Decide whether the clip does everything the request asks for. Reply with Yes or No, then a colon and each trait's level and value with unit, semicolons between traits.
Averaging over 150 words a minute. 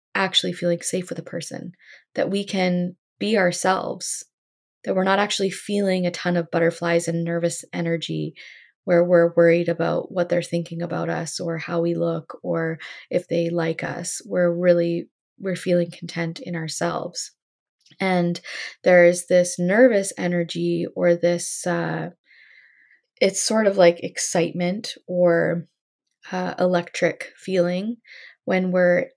No: average, 140 wpm